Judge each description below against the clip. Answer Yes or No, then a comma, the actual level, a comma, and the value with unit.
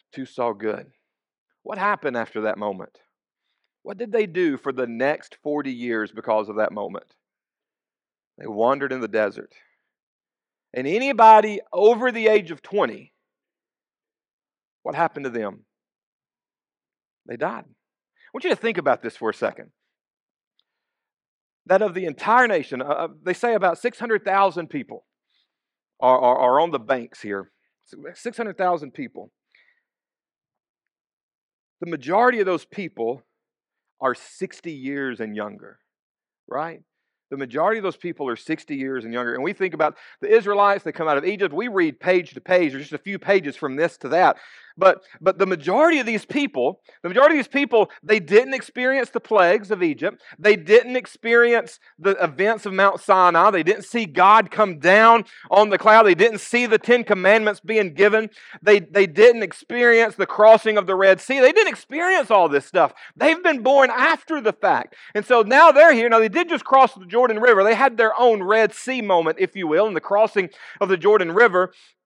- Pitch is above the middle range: Yes, high, 205 Hz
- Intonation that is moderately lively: No, wide, 5.9 semitones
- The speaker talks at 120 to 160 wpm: No, average, 175 wpm